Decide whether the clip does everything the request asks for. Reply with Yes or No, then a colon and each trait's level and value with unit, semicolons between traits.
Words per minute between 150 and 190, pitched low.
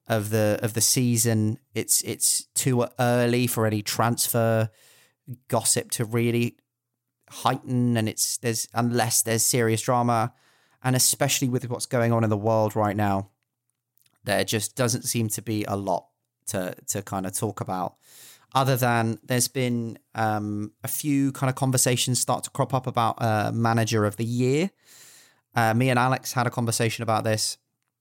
Yes: average, 165 wpm; low, 120 Hz